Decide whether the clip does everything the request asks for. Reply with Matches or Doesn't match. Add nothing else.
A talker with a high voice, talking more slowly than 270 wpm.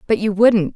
Matches